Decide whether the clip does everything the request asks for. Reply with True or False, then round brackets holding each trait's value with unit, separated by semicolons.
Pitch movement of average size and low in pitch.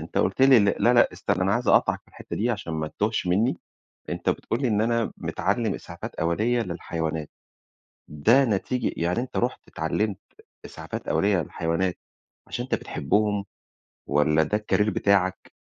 False (5.7 semitones; 100 Hz)